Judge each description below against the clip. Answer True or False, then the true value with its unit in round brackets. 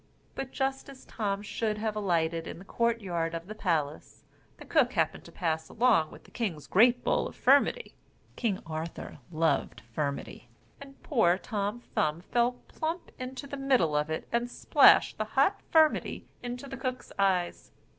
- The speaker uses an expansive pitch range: True (7.1 semitones)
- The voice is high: True (210 Hz)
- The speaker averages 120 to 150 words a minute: False (170 wpm)